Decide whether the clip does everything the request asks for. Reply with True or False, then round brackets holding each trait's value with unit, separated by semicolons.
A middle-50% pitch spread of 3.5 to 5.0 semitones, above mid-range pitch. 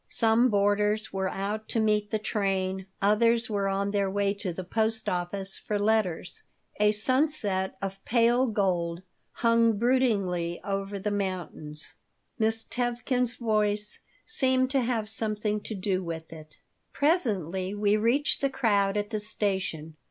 False (2.9 semitones; 210 Hz)